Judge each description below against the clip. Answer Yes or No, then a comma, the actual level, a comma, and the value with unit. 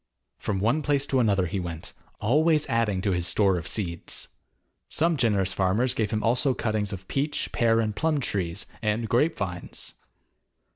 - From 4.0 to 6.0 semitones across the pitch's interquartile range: Yes, average, 5.0 semitones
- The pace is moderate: Yes, average, 165 wpm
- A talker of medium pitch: No, low, 110 Hz